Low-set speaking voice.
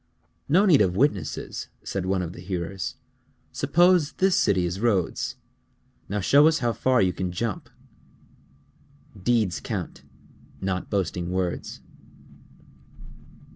Yes: low, 100 Hz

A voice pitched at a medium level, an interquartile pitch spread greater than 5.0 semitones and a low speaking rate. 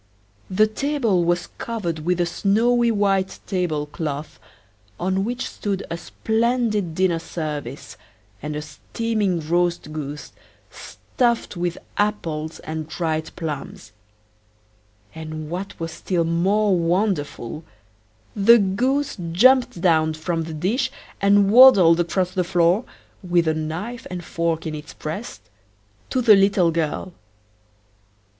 No: medium, 175 Hz; average, 4.5 semitones; slow, 125 wpm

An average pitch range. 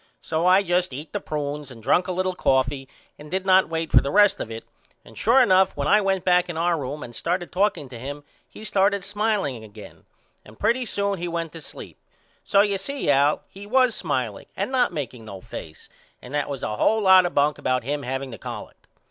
No: wide, 6.2 semitones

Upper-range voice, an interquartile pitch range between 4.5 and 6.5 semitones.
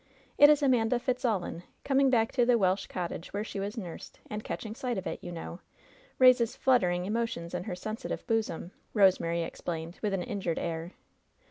Yes: high, 210 Hz; average, 5.3 semitones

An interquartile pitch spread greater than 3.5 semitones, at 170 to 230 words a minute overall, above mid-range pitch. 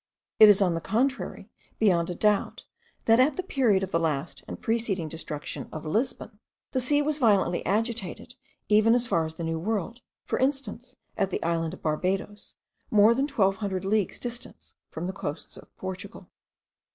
Yes: average, 5.1 semitones; average, 175 wpm; high, 205 Hz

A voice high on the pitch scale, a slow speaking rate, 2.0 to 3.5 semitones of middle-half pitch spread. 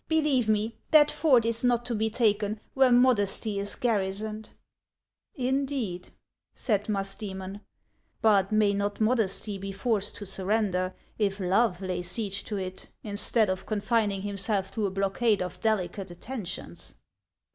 No: high, 210 Hz; average, 145 wpm; average, 2.8 semitones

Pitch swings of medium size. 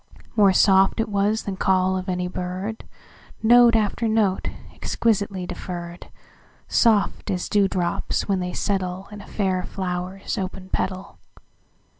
No: narrow, 2.0 semitones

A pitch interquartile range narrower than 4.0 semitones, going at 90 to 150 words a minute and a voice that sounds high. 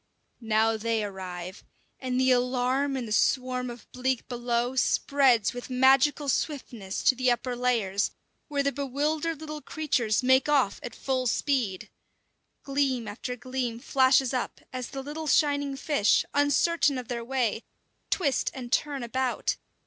Yes: average, 2.8 semitones; average, 145 wpm; very high, 255 Hz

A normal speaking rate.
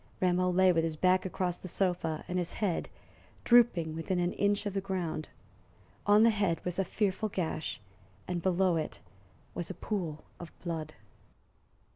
Yes: average, 165 wpm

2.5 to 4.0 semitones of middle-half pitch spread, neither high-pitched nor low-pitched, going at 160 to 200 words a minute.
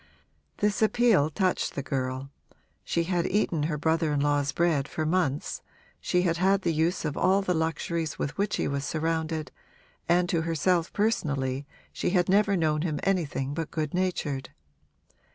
Yes: average, 3.6 semitones; medium, 165 Hz; average, 165 wpm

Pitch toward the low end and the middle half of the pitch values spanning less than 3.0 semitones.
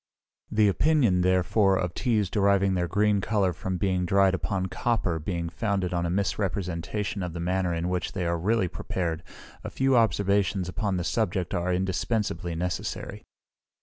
Yes: very low, 95 Hz; narrow, 2.5 semitones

